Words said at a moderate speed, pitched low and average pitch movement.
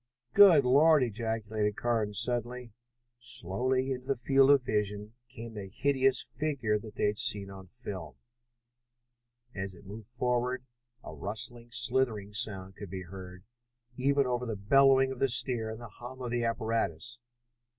Yes: average, 150 wpm; low, 120 Hz; average, 3.5 semitones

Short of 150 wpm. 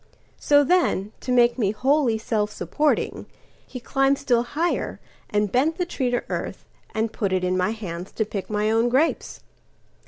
No: average, 160 wpm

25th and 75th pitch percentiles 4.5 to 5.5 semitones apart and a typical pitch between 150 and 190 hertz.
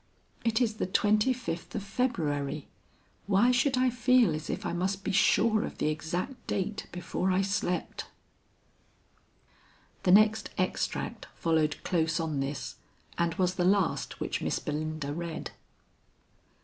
Yes: average, 5.2 semitones; medium, 185 Hz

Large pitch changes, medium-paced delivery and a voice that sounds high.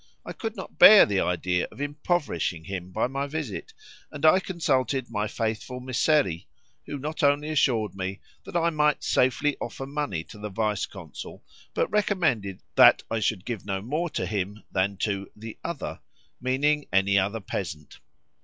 No: wide, 7.1 semitones; average, 165 wpm; low, 120 Hz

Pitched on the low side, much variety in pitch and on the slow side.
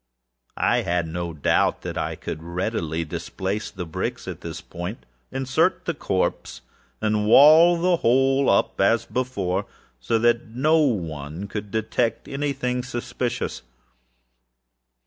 Yes: low, 110 Hz; wide, 6.8 semitones; slow, 130 wpm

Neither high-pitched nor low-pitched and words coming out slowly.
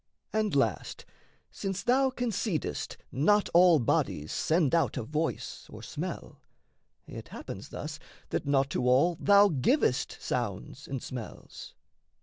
Yes: medium, 155 Hz; slow, 130 wpm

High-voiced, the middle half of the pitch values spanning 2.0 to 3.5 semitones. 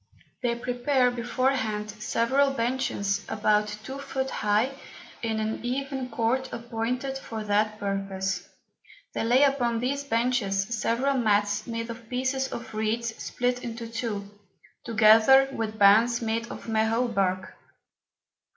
Yes: high, 230 Hz; average, 2.9 semitones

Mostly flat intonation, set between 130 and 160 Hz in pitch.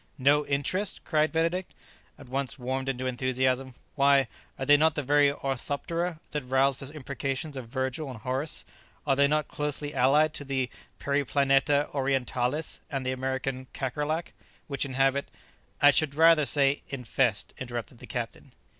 Yes: narrow, 2.1 semitones; medium, 140 Hz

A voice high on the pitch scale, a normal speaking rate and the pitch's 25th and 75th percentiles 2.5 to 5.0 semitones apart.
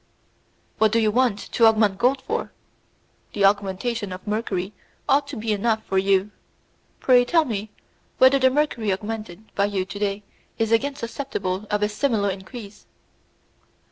Yes: high, 215 Hz; average, 155 wpm; average, 3.6 semitones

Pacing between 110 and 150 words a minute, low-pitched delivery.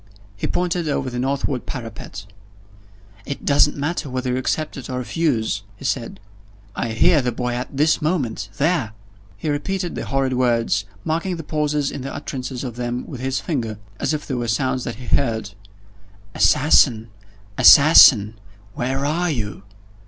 No: average, 160 wpm; low, 130 Hz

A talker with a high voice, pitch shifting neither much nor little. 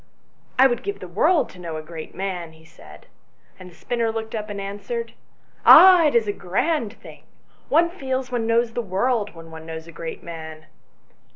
No: high, 205 Hz; wide, 7.0 semitones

